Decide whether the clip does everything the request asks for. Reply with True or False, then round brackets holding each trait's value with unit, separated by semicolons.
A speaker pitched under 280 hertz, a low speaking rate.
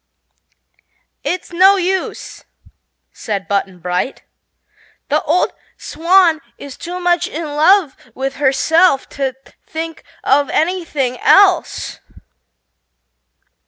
False (315 Hz; 90 wpm)